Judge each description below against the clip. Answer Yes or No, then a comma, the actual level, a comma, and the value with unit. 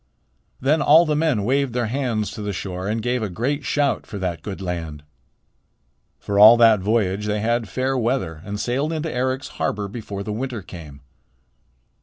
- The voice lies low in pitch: Yes, low, 110 Hz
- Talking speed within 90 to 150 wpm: No, average, 180 wpm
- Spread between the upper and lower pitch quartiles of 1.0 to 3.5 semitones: No, average, 4.7 semitones